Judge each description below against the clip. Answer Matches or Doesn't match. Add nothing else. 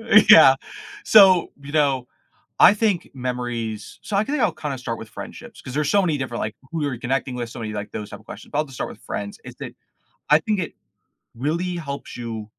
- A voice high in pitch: Doesn't match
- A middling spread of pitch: Doesn't match